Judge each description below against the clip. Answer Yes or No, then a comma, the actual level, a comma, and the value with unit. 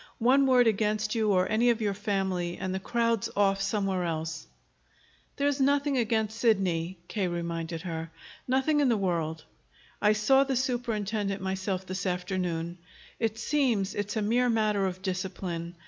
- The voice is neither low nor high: No, high, 200 Hz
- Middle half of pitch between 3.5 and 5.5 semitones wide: Yes, average, 4.0 semitones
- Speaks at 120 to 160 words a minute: Yes, average, 155 wpm